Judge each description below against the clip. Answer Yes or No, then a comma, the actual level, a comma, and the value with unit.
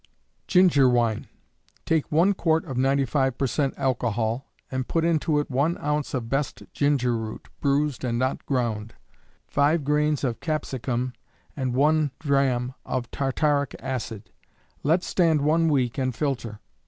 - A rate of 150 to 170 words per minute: No, average, 140 wpm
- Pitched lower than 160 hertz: Yes, low, 135 Hz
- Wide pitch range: No, average, 3.3 semitones